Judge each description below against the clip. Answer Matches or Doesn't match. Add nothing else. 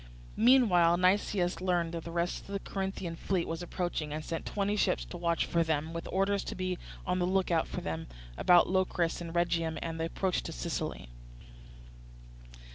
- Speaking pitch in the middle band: Matches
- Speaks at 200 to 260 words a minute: Doesn't match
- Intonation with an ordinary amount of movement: Doesn't match